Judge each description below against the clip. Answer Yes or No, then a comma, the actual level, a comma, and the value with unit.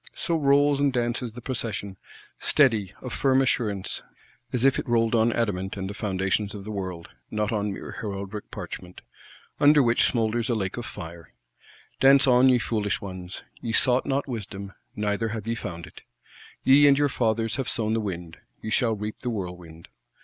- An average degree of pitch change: Yes, average, 4.1 semitones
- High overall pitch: No, low, 110 Hz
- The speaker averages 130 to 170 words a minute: No, average, 180 wpm